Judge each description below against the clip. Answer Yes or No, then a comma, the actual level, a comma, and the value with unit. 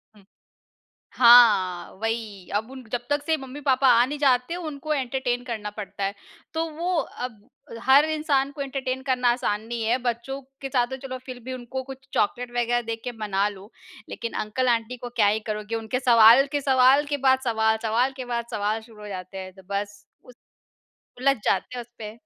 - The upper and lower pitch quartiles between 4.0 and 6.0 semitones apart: No, average, 3.3 semitones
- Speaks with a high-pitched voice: Yes, high, 245 Hz